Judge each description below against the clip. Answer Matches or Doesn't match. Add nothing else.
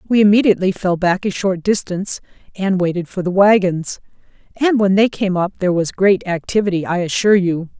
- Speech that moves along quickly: Doesn't match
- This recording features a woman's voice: Matches